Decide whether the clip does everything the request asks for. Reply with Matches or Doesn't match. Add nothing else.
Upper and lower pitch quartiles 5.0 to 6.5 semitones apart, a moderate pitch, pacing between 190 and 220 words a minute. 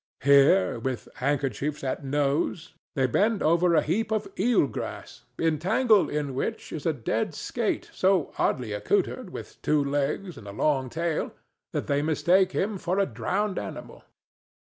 Doesn't match